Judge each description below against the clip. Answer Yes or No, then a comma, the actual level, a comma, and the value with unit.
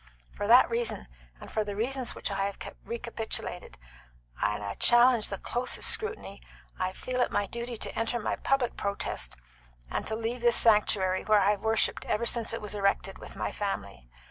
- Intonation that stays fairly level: No, average, 3.0 semitones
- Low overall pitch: No, high, 220 Hz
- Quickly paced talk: No, average, 185 wpm